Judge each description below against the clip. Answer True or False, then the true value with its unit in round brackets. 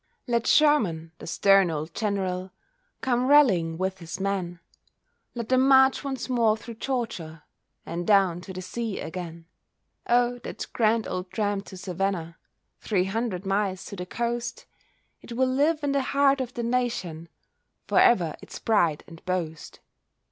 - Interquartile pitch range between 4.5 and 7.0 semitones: True (5.2 semitones)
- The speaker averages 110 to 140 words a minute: False (155 wpm)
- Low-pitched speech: False (200 Hz)